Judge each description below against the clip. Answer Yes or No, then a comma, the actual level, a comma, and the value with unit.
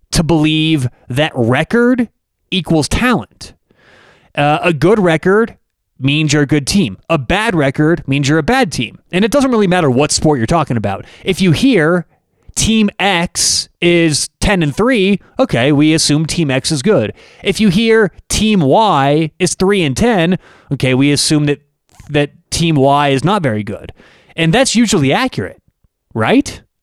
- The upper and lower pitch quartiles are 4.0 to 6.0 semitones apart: Yes, average, 5.2 semitones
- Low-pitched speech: No, medium, 160 Hz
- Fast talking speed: No, average, 165 wpm